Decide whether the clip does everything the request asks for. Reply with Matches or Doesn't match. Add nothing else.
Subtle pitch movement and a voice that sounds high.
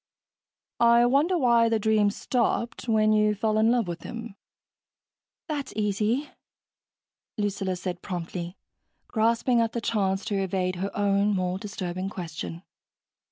Doesn't match